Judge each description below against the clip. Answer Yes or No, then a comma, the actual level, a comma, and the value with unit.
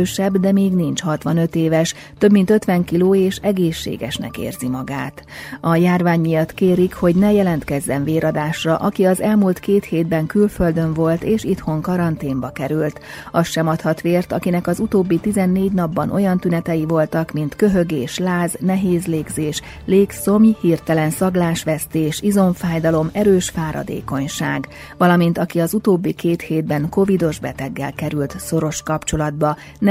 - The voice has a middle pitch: Yes, medium, 170 Hz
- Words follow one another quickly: No, average, 135 wpm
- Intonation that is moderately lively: Yes, average, 3.2 semitones